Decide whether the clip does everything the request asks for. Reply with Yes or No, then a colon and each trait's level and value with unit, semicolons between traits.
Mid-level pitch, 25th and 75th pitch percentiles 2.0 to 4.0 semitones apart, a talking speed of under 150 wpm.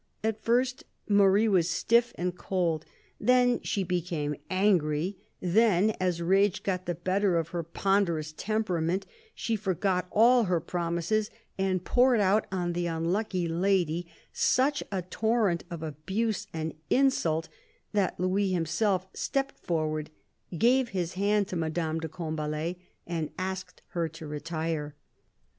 Yes: medium, 180 Hz; average, 3.7 semitones; slow, 135 wpm